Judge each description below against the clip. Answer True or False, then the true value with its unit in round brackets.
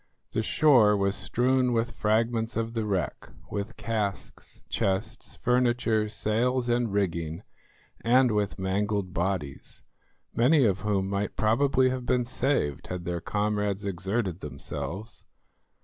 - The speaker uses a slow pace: True (125 wpm)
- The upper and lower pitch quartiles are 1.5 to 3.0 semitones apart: False (3.8 semitones)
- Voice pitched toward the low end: True (105 Hz)